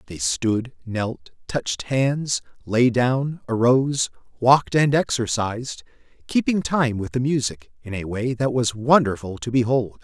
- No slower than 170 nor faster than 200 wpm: No, average, 145 wpm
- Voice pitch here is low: Yes, low, 125 Hz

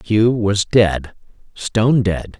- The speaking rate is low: Yes, slow, 125 wpm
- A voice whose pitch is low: Yes, low, 105 Hz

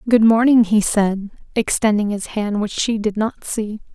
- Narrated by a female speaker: Yes, female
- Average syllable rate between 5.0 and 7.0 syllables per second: No, 4.4 syllables/s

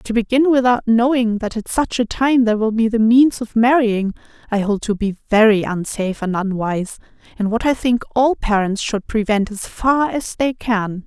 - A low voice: No, high, 225 Hz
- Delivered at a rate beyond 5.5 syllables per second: No, 4.9 syllables/s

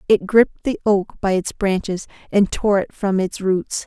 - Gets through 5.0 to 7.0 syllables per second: No, 4.4 syllables/s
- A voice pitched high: Yes, high, 195 Hz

